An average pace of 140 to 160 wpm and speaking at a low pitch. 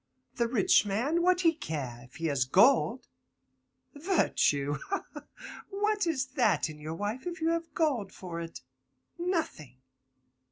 No: average, 150 wpm; high, 245 Hz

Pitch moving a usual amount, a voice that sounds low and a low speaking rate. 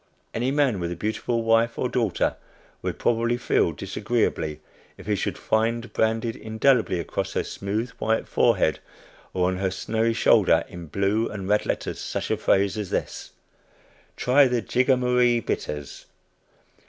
No: average, 3.6 semitones; low, 110 Hz; average, 150 wpm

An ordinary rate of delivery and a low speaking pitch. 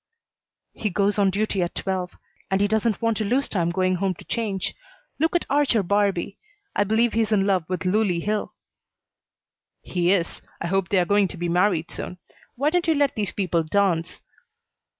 No: average, 190 wpm; high, 200 Hz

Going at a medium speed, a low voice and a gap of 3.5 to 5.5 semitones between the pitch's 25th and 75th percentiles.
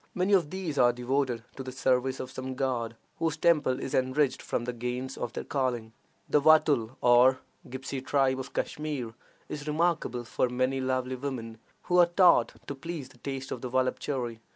No: average, 180 wpm; low, 130 Hz; average, 2.8 semitones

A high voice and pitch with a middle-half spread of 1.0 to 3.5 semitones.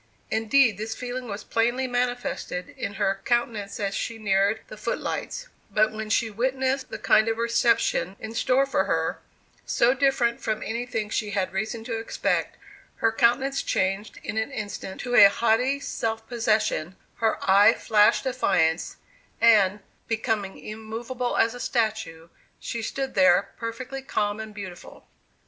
Yes: high, 225 Hz; average, 2.9 semitones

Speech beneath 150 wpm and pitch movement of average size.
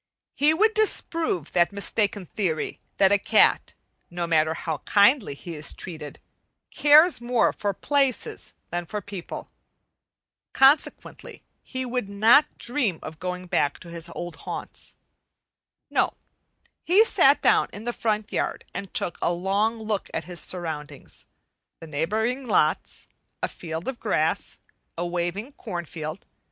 No: average, 140 wpm; wide, 6.0 semitones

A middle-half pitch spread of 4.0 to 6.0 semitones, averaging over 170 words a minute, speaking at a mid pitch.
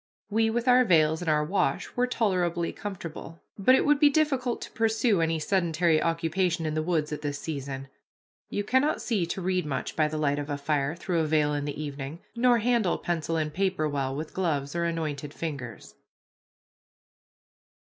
Yes: average, 4.7 semitones; average, 185 wpm; medium, 165 Hz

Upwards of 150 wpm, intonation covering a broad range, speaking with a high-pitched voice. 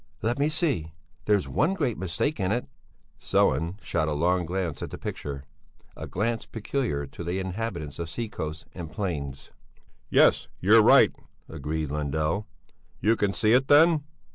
No: average, 160 wpm; wide, 6.8 semitones; very low, 95 Hz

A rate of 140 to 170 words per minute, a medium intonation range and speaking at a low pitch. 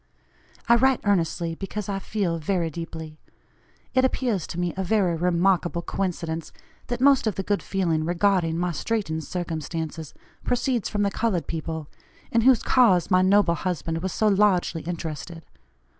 No: average, 155 wpm; average, 3.8 semitones; medium, 180 Hz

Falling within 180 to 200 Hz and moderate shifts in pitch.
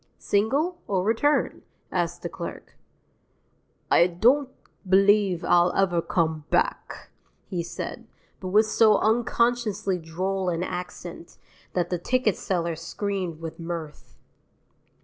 Yes: high, 190 Hz; average, 4.0 semitones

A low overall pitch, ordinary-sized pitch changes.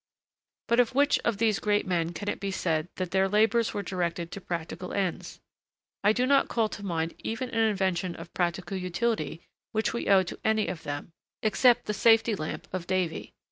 No: high, 195 Hz; average, 4.2 semitones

